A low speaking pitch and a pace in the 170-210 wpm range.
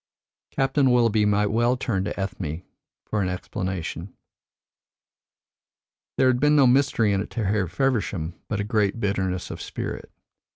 No: low, 105 Hz; average, 150 wpm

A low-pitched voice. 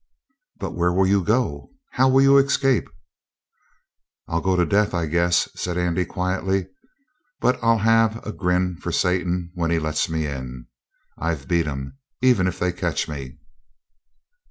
Yes: very low, 90 Hz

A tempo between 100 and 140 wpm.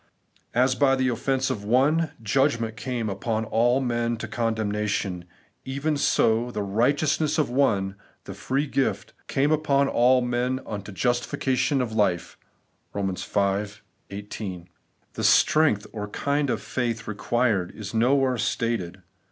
Yes: slow, 135 wpm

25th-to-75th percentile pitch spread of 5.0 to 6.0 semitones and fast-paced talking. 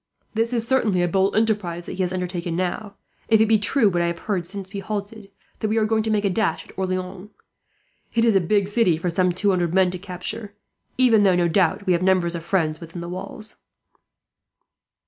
No: average, 3.2 semitones; fast, 220 wpm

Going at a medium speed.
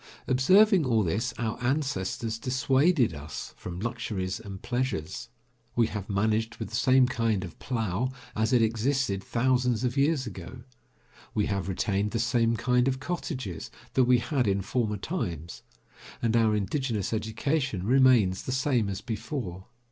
Yes: average, 150 wpm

